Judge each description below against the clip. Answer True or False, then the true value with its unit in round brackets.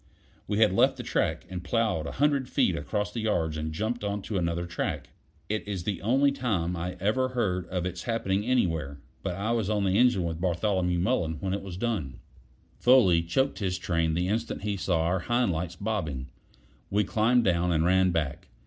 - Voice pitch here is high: False (95 Hz)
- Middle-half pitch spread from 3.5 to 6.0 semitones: True (4.2 semitones)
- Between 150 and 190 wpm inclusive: False (200 wpm)